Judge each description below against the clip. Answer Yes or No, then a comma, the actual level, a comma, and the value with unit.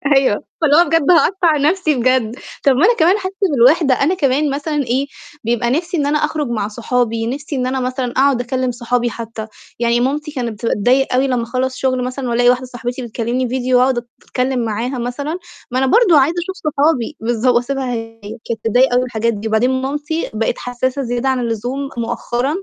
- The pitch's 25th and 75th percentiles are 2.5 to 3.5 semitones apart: Yes, average, 3.0 semitones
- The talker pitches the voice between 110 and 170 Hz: No, very high, 255 Hz